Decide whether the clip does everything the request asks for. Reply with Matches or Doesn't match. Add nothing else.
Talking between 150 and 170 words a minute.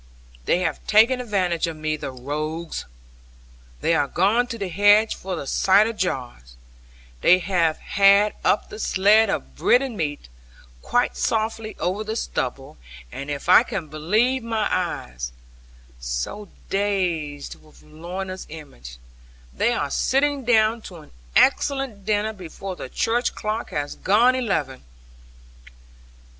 Doesn't match